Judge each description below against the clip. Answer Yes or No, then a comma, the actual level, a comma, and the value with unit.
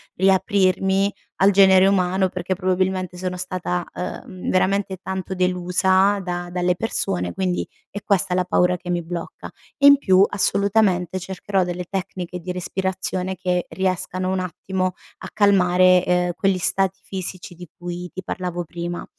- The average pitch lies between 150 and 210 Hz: Yes, medium, 185 Hz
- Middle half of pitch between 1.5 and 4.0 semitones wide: No, narrow, 1.1 semitones